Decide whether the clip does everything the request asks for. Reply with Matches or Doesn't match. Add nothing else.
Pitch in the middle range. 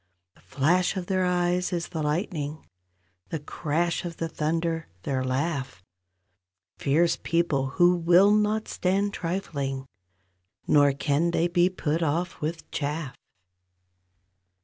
Matches